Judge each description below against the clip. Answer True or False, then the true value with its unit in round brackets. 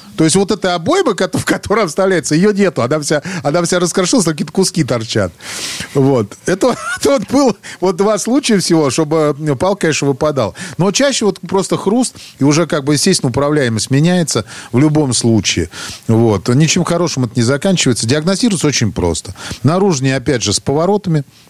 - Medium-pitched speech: True (160 Hz)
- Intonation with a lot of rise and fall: True (6.2 semitones)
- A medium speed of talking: False (170 wpm)